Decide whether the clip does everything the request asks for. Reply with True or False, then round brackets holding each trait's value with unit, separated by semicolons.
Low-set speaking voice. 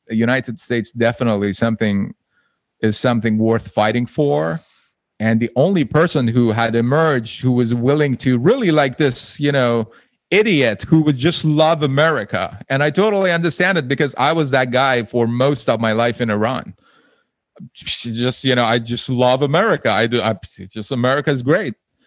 True (125 Hz)